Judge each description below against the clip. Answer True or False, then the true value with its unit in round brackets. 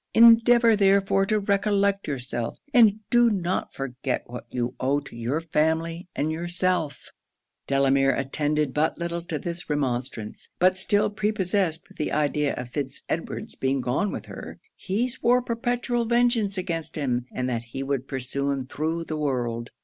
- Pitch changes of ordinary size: False (6.8 semitones)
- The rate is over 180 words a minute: False (155 wpm)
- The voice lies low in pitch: False (160 Hz)